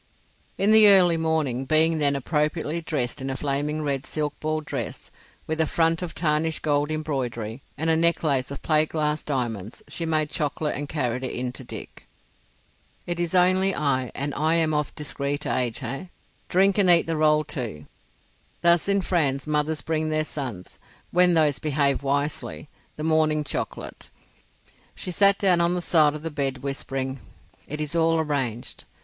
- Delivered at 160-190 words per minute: Yes, average, 170 wpm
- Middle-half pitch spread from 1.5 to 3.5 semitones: Yes, average, 2.8 semitones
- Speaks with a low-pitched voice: No, medium, 150 Hz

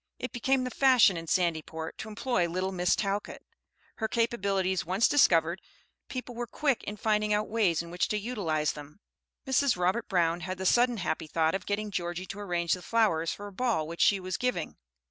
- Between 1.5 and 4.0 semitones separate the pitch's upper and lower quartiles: No, average, 5.0 semitones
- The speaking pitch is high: Yes, high, 195 Hz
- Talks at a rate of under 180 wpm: No, average, 195 wpm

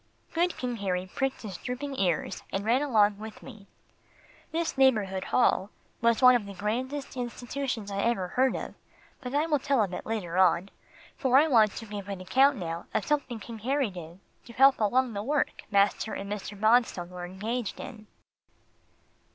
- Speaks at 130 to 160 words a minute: No, average, 180 wpm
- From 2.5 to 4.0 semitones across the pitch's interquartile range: No, average, 4.7 semitones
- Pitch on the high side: Yes, high, 225 Hz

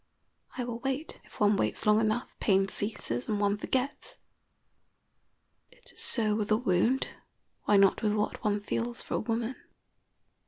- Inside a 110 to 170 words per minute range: Yes, average, 160 wpm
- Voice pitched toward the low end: No, high, 215 Hz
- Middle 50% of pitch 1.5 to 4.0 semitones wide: Yes, average, 2.8 semitones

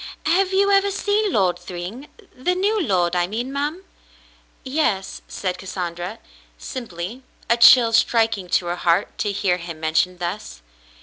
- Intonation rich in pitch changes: Yes, wide, 8.9 semitones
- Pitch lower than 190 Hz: No, high, 210 Hz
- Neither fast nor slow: Yes, average, 160 wpm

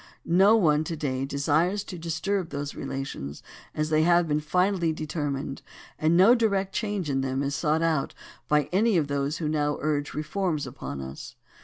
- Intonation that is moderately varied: Yes, average, 4.0 semitones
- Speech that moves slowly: No, average, 170 wpm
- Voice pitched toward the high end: No, medium, 155 Hz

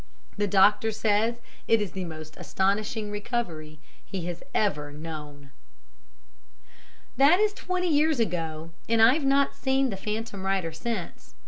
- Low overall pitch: No, high, 205 Hz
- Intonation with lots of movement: Yes, wide, 6.2 semitones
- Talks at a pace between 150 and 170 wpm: No, slow, 135 wpm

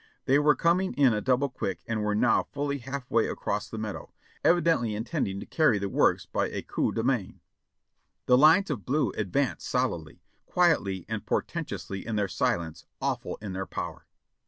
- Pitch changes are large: Yes, wide, 6.2 semitones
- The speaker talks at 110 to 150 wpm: No, average, 180 wpm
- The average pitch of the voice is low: Yes, low, 120 Hz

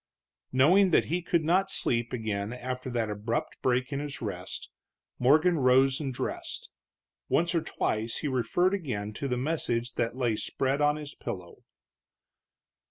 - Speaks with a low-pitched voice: Yes, low, 130 Hz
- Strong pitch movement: No, average, 4.7 semitones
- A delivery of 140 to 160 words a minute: Yes, average, 155 wpm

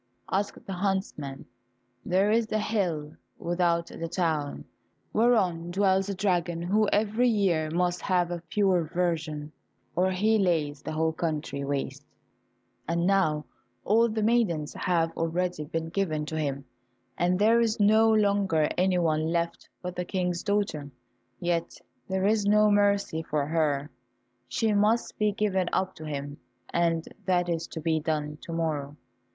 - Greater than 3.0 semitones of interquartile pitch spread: Yes, average, 4.2 semitones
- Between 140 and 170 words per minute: Yes, average, 150 wpm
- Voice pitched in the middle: Yes, medium, 175 Hz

